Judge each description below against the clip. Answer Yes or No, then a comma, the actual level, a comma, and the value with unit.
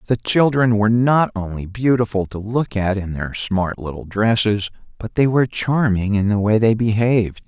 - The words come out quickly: No, average, 185 wpm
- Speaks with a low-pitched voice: Yes, low, 110 Hz